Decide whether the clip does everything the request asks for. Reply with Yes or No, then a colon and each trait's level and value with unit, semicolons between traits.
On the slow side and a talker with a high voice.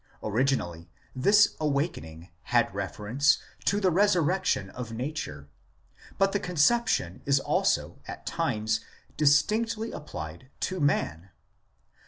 No: slow, 105 wpm; medium, 140 Hz